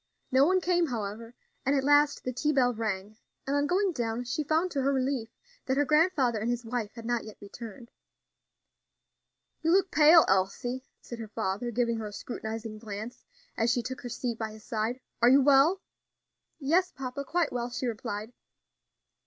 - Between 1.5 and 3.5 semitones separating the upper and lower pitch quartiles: No, average, 4.2 semitones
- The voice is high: Yes, high, 245 Hz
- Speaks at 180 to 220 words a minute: Yes, average, 185 wpm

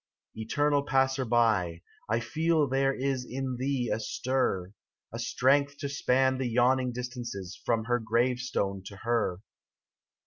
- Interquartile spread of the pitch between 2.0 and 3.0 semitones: Yes, average, 2.7 semitones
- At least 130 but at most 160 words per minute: Yes, average, 140 wpm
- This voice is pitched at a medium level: No, low, 125 Hz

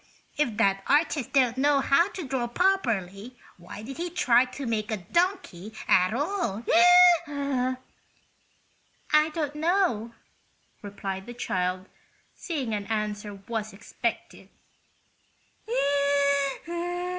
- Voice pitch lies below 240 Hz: No, high, 245 Hz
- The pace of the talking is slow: Yes, slow, 105 wpm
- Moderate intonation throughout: No, wide, 6.1 semitones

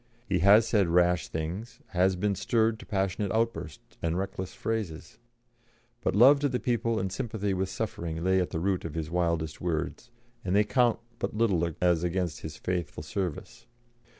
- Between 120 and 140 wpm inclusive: No, average, 175 wpm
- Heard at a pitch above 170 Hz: No, very low, 95 Hz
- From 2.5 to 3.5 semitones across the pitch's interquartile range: No, average, 4.5 semitones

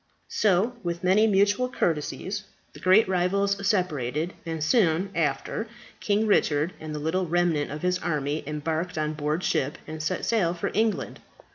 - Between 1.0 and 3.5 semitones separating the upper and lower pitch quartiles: No, average, 4.4 semitones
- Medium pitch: Yes, medium, 175 Hz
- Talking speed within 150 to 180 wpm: Yes, average, 155 wpm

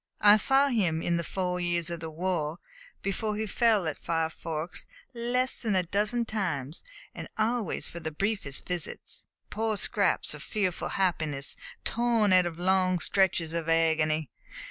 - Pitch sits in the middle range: Yes, medium, 180 Hz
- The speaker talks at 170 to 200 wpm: No, average, 160 wpm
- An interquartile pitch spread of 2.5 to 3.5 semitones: No, average, 4.6 semitones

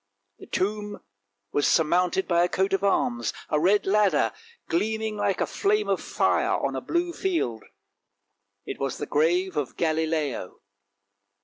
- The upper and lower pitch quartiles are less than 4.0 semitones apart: No, average, 5.1 semitones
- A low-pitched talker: No, medium, 180 Hz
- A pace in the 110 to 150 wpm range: Yes, average, 145 wpm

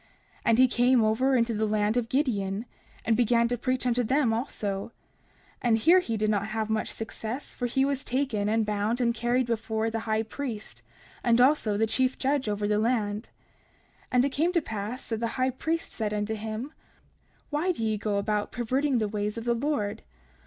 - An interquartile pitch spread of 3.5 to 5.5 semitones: No, average, 3.0 semitones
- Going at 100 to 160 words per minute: No, average, 200 wpm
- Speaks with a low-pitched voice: No, high, 230 Hz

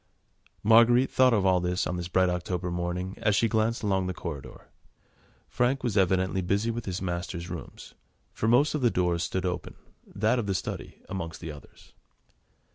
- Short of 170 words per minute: No, average, 180 wpm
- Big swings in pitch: No, average, 4.0 semitones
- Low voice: Yes, very low, 95 Hz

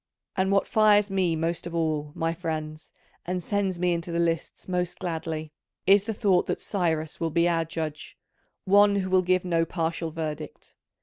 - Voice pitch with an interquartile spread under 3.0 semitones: Yes, narrow, 2.5 semitones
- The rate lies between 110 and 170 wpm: No, average, 180 wpm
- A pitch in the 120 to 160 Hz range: No, medium, 170 Hz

